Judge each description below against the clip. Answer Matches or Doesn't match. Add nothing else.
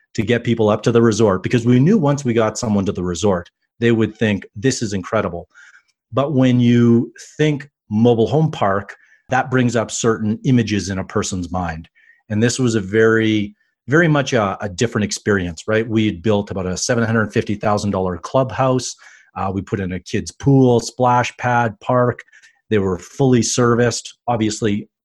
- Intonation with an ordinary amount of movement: Matches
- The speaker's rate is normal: Matches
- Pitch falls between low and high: Doesn't match